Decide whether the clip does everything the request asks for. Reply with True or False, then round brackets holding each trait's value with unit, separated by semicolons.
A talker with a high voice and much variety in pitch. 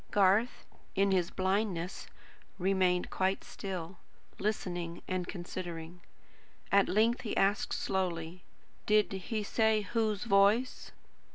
False (195 Hz; 2.7 semitones)